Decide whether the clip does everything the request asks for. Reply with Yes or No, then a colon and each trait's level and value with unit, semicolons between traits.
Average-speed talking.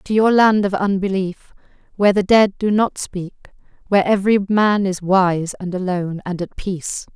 Yes: average, 170 wpm